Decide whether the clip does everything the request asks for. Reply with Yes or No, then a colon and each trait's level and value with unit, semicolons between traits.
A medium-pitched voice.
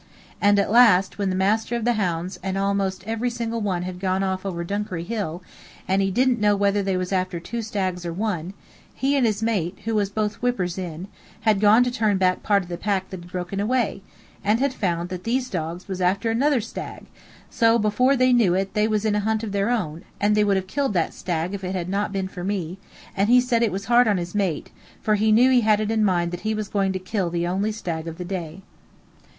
No: high, 200 Hz